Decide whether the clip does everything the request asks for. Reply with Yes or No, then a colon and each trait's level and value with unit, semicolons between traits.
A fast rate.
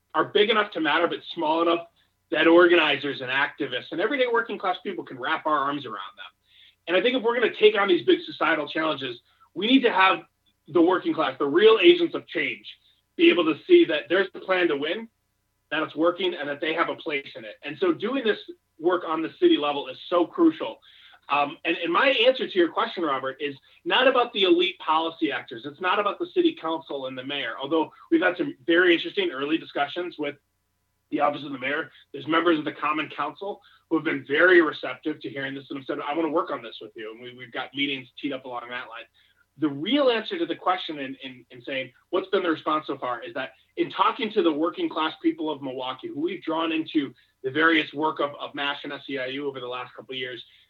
Yes: fast, 235 wpm